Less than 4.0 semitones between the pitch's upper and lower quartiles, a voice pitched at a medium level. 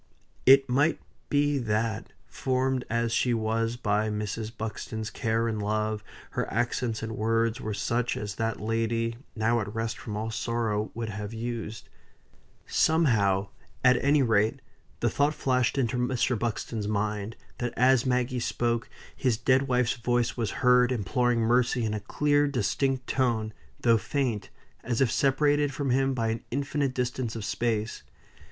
No: narrow, 2.6 semitones; low, 115 Hz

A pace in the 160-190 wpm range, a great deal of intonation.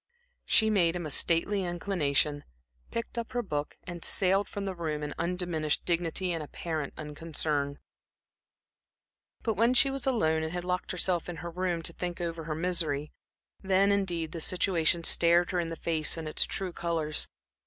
No: average, 175 wpm; average, 2.8 semitones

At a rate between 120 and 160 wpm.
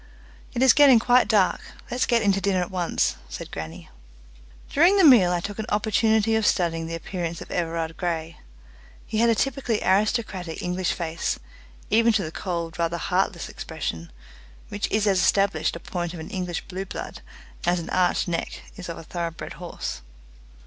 No: average, 180 wpm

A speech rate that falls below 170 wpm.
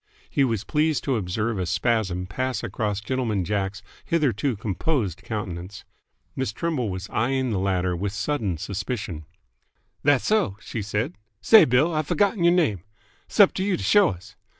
Yes: average, 155 wpm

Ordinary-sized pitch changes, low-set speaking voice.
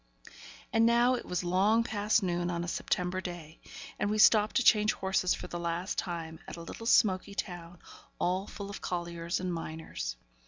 No: average, 3.3 semitones; medium, 180 Hz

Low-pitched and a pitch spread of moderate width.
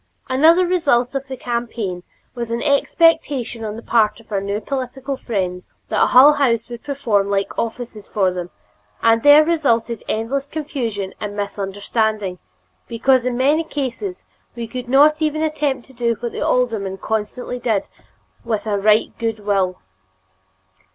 No: high, 235 Hz; average, 4.6 semitones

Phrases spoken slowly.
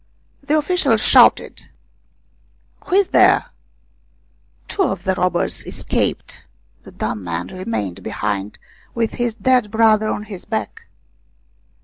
Yes: slow, 125 wpm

